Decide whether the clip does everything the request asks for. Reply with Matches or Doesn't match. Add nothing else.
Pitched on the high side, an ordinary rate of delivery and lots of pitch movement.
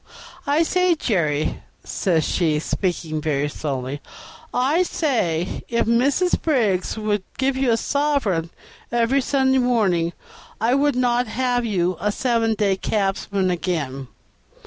Doesn't match